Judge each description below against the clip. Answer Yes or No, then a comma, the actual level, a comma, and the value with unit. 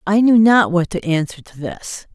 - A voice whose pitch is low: No, high, 190 Hz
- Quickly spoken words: Yes, fast, 225 wpm